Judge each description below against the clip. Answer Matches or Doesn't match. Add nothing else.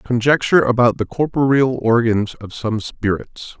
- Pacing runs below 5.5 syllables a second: Matches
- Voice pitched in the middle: Doesn't match